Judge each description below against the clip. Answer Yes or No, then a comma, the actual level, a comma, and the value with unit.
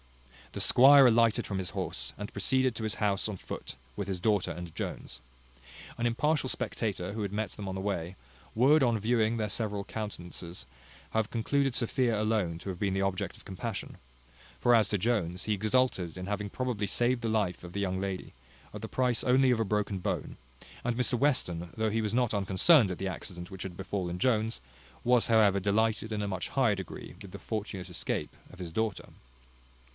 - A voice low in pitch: Yes, low, 105 Hz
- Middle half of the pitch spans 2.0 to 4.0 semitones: Yes, average, 3.6 semitones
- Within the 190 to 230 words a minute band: Yes, average, 200 wpm